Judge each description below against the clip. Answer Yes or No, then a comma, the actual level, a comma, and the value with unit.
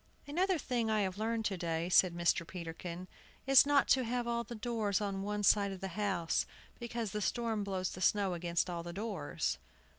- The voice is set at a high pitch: Yes, high, 200 Hz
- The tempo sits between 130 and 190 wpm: No, average, 200 wpm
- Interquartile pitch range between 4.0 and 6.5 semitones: Yes, average, 4.5 semitones